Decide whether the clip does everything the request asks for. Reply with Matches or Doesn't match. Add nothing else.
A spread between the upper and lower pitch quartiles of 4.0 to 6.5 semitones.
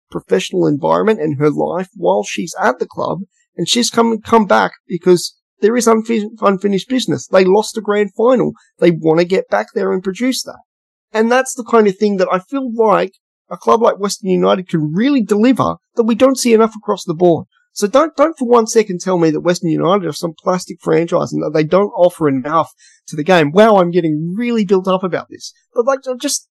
Matches